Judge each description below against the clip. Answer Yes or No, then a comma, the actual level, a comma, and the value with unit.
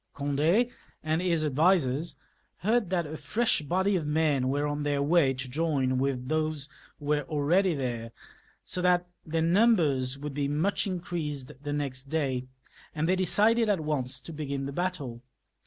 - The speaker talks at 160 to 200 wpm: Yes, average, 165 wpm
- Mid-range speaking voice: Yes, medium, 150 Hz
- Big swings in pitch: No, average, 4.1 semitones